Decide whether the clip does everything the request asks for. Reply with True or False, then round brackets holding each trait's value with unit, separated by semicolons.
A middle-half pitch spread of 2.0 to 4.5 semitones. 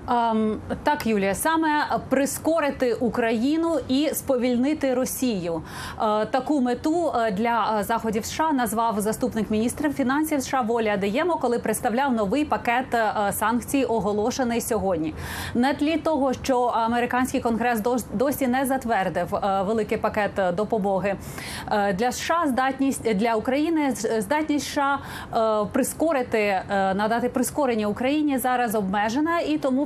True (3.8 semitones)